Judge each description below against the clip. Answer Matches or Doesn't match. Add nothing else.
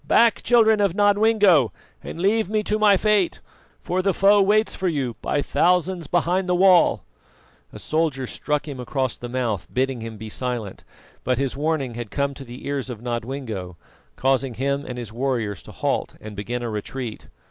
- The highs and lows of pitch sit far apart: Matches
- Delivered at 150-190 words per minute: Matches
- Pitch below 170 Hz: Matches